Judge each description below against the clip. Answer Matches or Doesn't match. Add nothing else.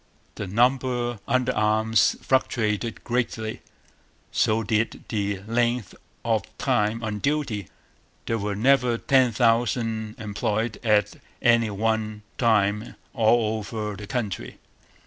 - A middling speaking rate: Doesn't match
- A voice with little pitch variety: Matches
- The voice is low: Matches